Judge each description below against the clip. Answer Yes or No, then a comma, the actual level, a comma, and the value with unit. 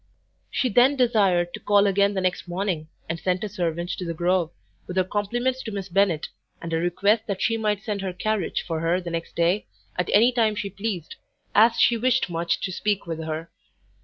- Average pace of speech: No, fast, 215 wpm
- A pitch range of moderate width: Yes, average, 3.6 semitones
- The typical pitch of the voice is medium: No, high, 195 Hz